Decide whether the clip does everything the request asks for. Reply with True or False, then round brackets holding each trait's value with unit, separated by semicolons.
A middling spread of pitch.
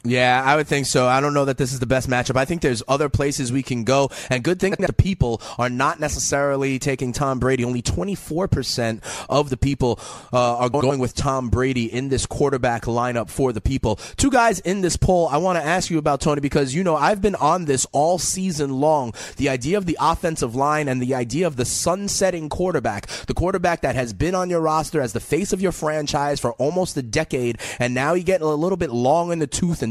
True (4.6 semitones)